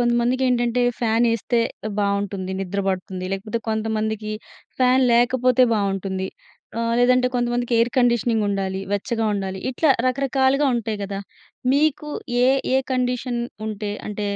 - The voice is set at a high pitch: Yes, high, 230 Hz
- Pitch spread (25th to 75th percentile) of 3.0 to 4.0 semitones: Yes, average, 3.6 semitones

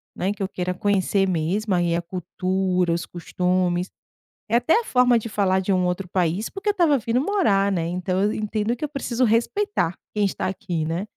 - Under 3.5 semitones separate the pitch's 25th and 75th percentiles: No, average, 4.2 semitones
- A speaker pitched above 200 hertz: No, high, 195 Hz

